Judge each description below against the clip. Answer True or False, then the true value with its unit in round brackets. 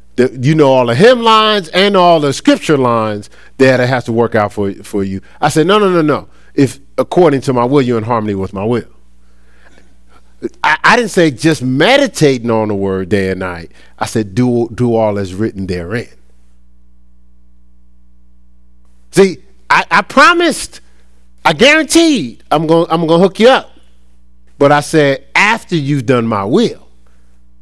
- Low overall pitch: True (115 Hz)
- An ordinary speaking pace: True (170 wpm)